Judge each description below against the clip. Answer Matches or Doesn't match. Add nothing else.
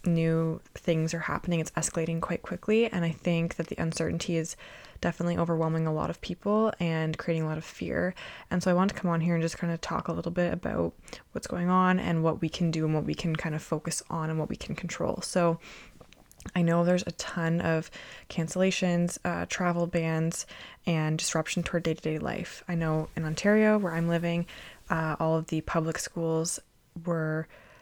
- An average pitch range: Doesn't match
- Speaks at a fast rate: Matches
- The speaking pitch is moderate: Matches